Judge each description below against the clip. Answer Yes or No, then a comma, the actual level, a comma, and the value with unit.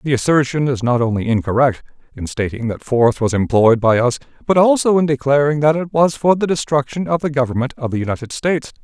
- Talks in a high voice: No, low, 135 Hz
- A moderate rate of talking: No, fast, 210 wpm